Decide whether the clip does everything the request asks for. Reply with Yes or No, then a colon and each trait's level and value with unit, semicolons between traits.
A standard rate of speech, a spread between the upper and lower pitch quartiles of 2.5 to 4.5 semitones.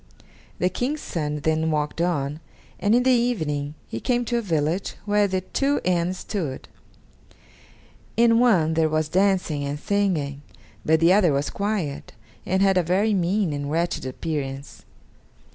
No: average, 155 wpm; average, 5.2 semitones